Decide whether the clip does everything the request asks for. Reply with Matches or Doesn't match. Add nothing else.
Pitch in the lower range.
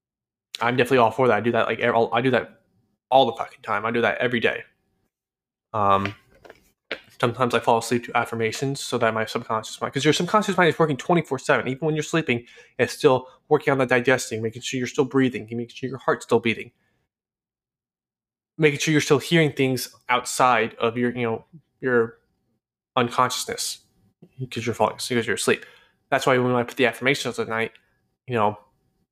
Matches